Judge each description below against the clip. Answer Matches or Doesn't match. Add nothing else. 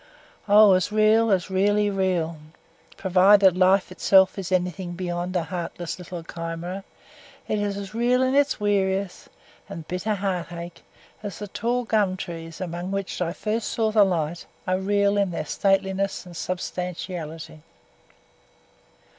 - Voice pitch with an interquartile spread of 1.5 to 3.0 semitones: Matches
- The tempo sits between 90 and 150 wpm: Matches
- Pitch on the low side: Doesn't match